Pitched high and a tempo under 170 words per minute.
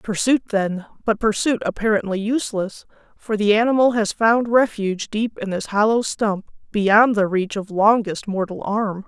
Yes: high, 210 Hz; average, 160 wpm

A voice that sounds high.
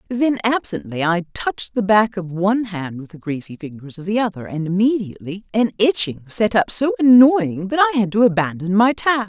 Yes: high, 200 Hz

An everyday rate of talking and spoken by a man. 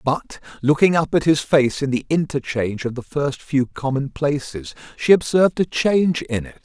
Yes: average, 190 wpm; male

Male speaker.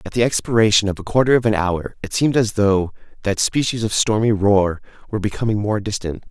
Yes: male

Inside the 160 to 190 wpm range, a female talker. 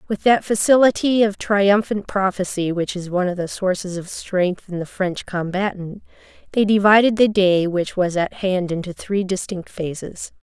Yes: average, 175 wpm; female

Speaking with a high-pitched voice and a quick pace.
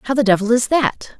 Yes: high, 240 Hz; fast, 250 wpm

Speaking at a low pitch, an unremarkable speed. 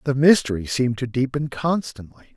Yes: low, 130 Hz; average, 155 wpm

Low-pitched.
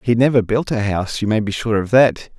Yes: low, 110 Hz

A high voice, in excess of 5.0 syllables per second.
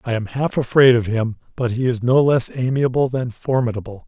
No: low, 125 Hz; 5.4 syllables/s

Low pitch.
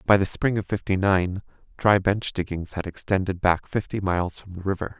Yes: very low, 95 Hz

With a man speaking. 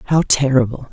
Yes: male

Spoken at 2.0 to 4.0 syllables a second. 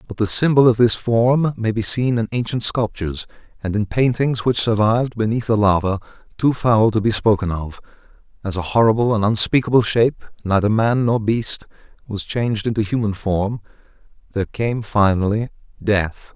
No: 5.2 syllables/s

